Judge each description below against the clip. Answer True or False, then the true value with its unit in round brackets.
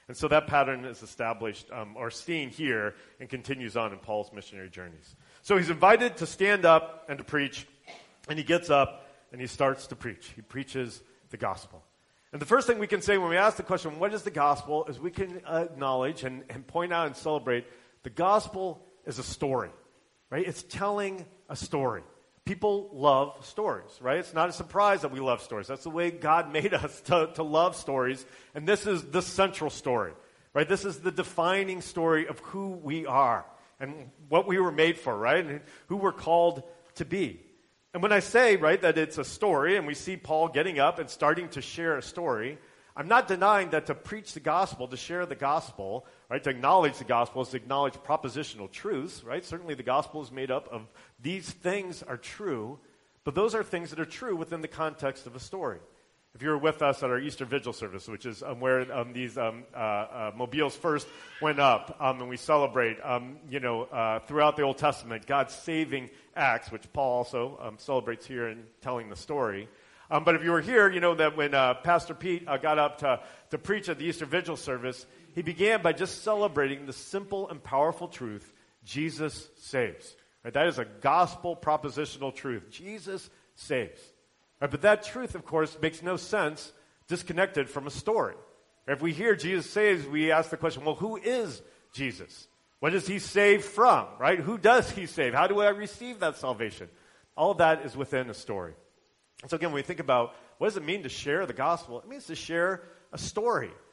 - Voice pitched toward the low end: False (155 Hz)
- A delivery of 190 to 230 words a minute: True (205 wpm)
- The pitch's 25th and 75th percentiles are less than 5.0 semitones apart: False (5.4 semitones)